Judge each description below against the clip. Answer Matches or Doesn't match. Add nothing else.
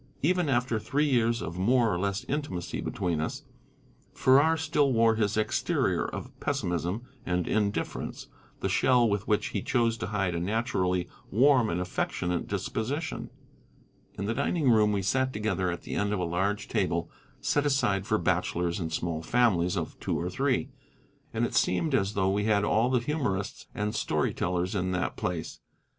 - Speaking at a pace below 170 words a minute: Doesn't match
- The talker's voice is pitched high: Doesn't match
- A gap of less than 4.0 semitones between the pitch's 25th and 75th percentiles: Doesn't match